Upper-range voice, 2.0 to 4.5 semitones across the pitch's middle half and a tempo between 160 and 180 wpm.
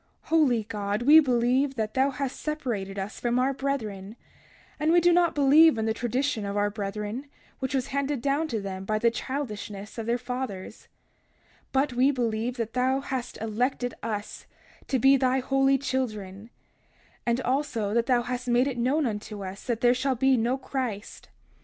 Yes: high, 245 Hz; average, 3.7 semitones; average, 175 wpm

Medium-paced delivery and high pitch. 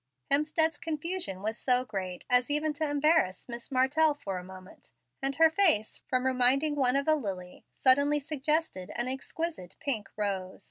Yes: average, 165 wpm; very high, 265 Hz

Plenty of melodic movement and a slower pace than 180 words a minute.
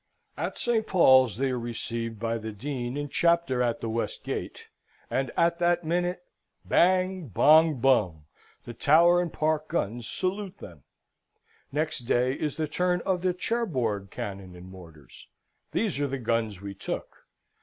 Yes: wide, 7.1 semitones; average, 155 wpm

